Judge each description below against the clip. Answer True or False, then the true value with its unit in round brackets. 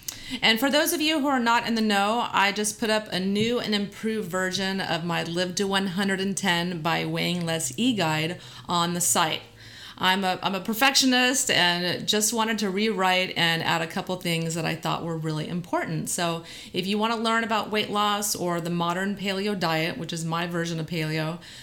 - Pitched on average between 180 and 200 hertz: True (190 Hz)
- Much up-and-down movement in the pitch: False (4.2 semitones)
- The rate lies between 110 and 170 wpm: False (205 wpm)